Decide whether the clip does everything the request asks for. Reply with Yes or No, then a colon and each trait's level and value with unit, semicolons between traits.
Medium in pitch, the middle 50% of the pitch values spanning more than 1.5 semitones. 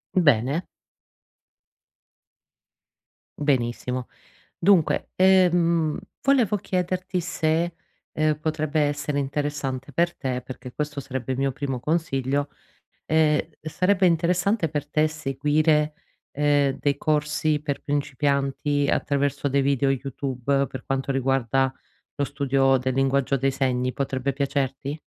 Yes: medium, 145 Hz; narrow, 2.5 semitones